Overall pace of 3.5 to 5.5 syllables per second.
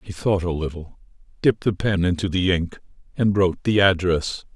Yes: 5.4 syllables/s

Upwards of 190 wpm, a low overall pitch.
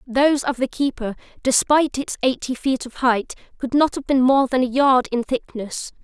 No: average, 200 wpm; very high, 260 Hz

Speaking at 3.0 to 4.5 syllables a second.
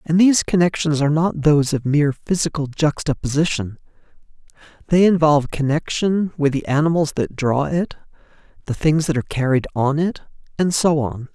No: 5.5 syllables/s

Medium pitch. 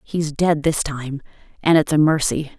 Yes: medium, 150 Hz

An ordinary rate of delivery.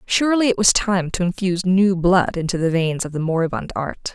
No: fast, 215 wpm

